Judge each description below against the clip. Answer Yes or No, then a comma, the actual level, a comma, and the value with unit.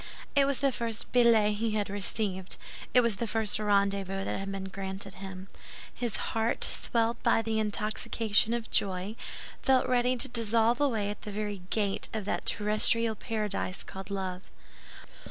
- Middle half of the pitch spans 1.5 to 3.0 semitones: Yes, average, 2.7 semitones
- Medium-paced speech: Yes, average, 160 wpm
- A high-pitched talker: Yes, high, 215 Hz